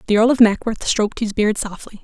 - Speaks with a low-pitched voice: No, high, 215 Hz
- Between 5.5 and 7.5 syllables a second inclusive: Yes, 6.0 syllables/s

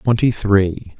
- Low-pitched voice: Yes, low, 100 Hz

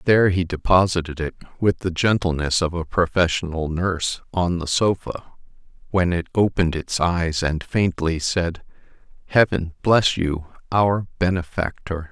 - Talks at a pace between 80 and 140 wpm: Yes, slow, 135 wpm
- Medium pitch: No, very low, 85 Hz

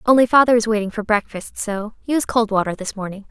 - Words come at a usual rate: No, fast, 220 wpm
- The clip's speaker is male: No, female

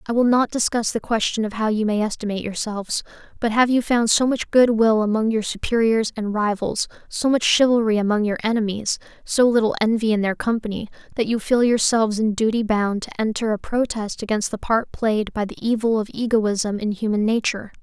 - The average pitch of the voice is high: Yes, high, 220 Hz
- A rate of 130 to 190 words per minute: No, average, 200 wpm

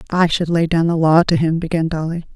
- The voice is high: No, medium, 165 Hz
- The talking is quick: Yes, fast, 255 wpm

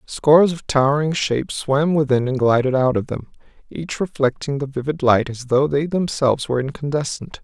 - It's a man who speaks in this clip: Yes, male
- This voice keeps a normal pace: Yes, average, 180 wpm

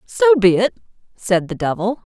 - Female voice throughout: Yes, female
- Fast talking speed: No, average, 170 wpm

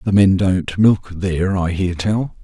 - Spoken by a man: Yes, male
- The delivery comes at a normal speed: Yes, average, 195 wpm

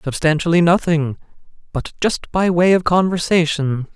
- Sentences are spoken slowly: Yes, slow, 105 wpm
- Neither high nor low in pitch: Yes, medium, 165 Hz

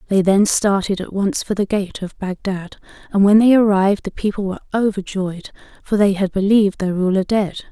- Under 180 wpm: No, average, 195 wpm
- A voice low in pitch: No, high, 200 Hz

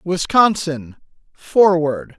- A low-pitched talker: No, medium, 170 Hz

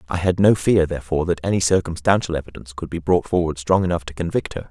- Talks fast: Yes, fast, 230 wpm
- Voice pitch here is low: Yes, very low, 85 Hz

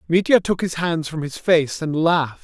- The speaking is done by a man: Yes, male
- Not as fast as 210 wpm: No, fast, 220 wpm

